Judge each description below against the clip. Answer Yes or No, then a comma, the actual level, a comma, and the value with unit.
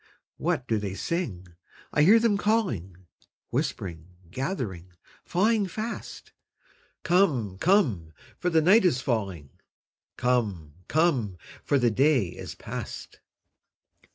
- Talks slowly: Yes, slow, 110 wpm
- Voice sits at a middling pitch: No, low, 125 Hz